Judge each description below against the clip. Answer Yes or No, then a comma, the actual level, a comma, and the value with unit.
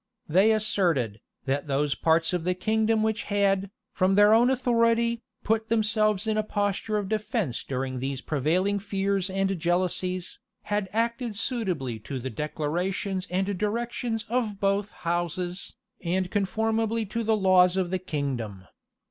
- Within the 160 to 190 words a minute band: No, average, 145 wpm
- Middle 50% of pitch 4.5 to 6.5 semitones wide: No, average, 4.0 semitones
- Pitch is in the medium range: No, high, 195 Hz